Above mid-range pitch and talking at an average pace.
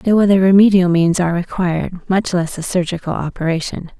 No: medium, 180 Hz; average, 165 wpm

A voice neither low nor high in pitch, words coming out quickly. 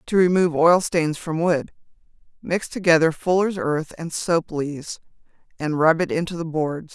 No: medium, 165 Hz; average, 155 wpm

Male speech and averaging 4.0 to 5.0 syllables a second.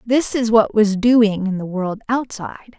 No: female; 4.6 syllables/s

